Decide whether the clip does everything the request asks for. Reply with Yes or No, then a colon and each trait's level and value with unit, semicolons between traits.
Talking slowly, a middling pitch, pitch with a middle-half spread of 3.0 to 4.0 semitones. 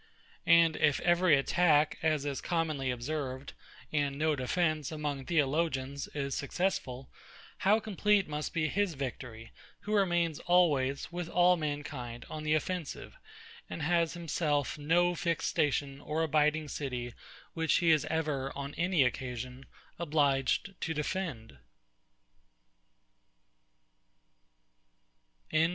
Yes: slow, 115 wpm; medium, 150 Hz; average, 3.5 semitones